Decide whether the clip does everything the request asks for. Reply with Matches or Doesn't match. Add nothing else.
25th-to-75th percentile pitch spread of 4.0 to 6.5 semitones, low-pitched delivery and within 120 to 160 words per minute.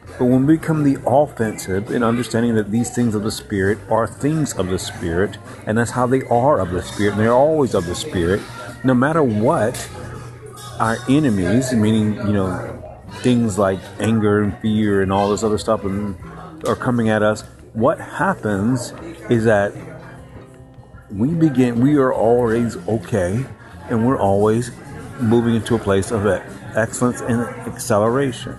Doesn't match